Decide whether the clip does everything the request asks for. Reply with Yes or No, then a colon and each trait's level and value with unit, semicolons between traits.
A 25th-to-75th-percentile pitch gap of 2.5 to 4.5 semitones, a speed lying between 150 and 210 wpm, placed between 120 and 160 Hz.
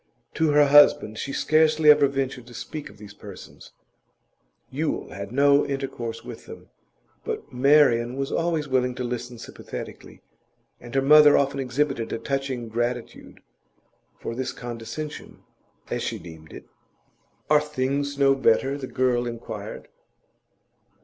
No: average, 3.2 semitones; slow, 135 wpm; low, 135 Hz